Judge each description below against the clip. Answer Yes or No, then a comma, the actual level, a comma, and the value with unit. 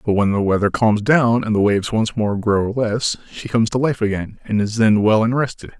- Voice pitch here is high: No, low, 110 Hz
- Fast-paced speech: Yes, fast, 250 wpm